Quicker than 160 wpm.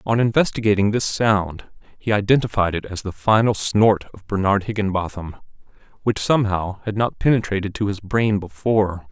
No: average, 150 wpm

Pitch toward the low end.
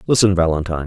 Yes: very low, 90 Hz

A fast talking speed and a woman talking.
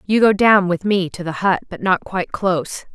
Yes: fast, 245 wpm; female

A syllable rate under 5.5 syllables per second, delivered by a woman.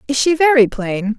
Yes: 5.0 syllables/s; female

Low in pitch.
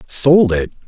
Yes: low, 125 Hz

